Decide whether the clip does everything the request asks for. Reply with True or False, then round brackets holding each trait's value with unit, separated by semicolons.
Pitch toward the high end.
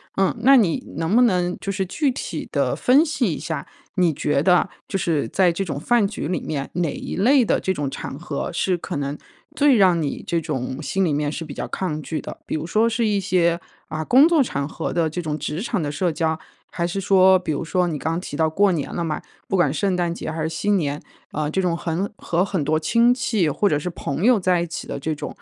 False (175 Hz)